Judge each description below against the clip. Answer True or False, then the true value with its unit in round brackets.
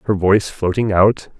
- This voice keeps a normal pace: True (170 wpm)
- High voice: False (100 Hz)